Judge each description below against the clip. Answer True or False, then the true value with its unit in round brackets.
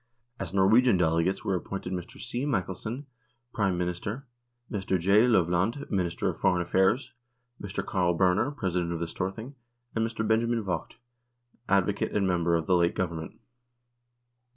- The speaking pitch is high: False (95 Hz)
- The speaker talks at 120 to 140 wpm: False (150 wpm)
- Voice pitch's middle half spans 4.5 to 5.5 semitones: False (3.8 semitones)